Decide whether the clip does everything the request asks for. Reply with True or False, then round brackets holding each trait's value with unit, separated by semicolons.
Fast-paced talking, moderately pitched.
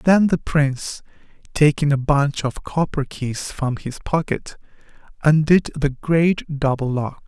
False (140 wpm; 145 Hz)